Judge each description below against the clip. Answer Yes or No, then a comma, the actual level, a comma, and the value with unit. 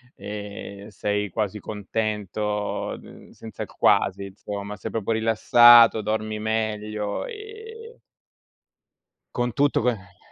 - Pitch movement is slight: Yes, narrow, 1.9 semitones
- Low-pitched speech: Yes, low, 110 Hz